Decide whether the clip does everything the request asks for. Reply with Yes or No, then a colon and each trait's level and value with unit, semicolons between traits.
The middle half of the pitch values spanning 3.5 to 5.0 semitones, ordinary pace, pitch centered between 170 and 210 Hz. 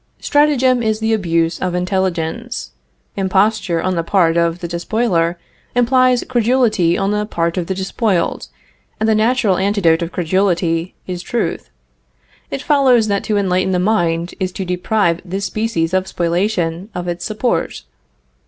Yes: average, 4.1 semitones; average, 150 wpm; high, 190 Hz